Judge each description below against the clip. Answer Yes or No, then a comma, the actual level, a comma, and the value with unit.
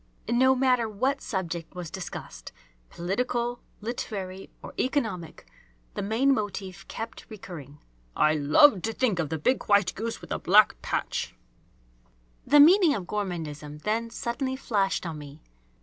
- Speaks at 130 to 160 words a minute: Yes, average, 140 wpm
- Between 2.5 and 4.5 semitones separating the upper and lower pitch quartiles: No, wide, 5.6 semitones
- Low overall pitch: No, high, 205 Hz